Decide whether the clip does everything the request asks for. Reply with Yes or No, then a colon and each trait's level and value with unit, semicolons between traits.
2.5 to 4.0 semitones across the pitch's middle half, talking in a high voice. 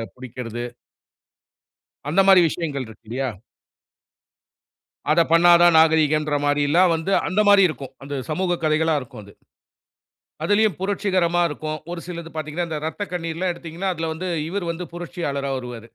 No: average, 3.4 semitones; medium, 160 Hz